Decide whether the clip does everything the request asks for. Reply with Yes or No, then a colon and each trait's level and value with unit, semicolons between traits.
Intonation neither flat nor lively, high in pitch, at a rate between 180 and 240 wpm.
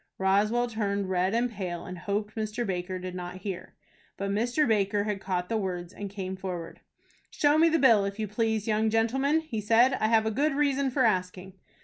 Yes: average, 3.5 semitones; high, 210 Hz; fast, 205 wpm